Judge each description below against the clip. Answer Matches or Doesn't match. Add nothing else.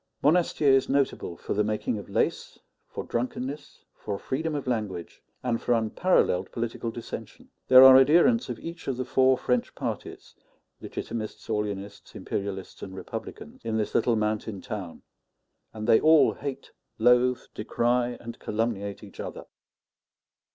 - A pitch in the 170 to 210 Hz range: Doesn't match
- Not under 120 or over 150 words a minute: Matches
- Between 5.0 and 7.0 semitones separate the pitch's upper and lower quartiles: Doesn't match